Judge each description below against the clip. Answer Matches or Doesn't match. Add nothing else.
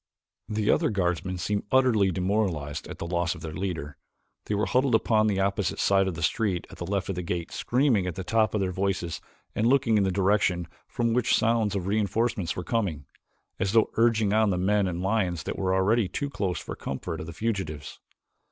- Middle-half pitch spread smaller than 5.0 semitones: Matches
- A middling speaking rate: Doesn't match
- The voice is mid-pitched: Doesn't match